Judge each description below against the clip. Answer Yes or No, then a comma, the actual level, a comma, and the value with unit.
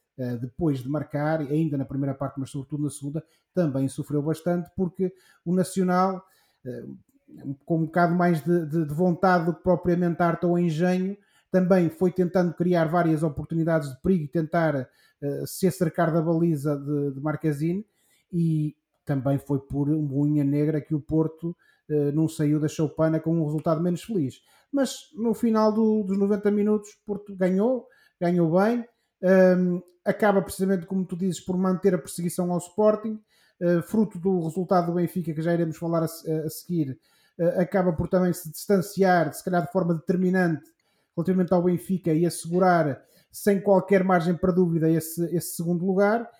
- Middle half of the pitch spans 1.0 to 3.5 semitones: Yes, average, 2.9 semitones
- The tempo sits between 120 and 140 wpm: No, average, 165 wpm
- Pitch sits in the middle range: Yes, medium, 175 Hz